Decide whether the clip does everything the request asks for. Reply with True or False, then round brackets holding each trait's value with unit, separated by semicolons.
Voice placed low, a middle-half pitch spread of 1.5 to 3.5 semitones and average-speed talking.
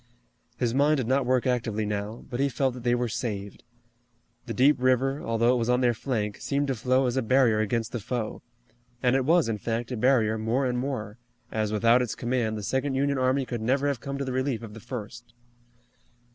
False (125 Hz; 2.8 semitones; 220 wpm)